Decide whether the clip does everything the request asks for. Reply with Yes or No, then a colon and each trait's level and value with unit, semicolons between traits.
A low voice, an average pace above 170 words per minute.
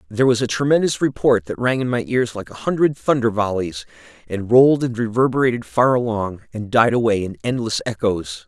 Yes: low, 120 Hz; average, 190 wpm